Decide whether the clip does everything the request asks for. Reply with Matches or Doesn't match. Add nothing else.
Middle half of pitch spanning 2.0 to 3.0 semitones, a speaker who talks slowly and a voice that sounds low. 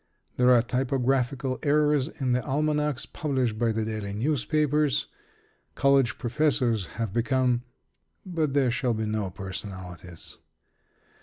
Doesn't match